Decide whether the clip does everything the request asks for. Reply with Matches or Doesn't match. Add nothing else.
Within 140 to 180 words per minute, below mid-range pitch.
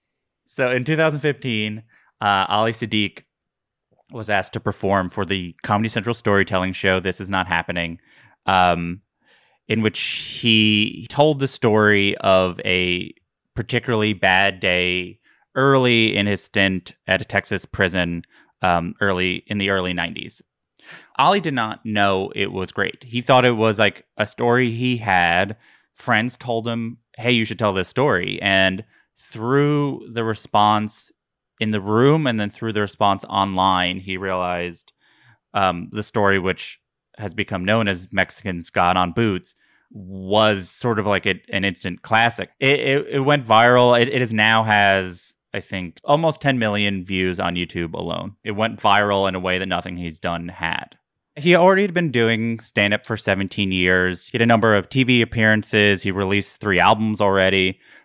Matches